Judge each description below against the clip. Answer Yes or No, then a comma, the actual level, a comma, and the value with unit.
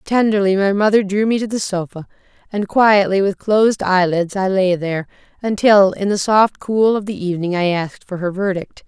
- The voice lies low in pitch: No, high, 195 Hz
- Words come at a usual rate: Yes, average, 195 wpm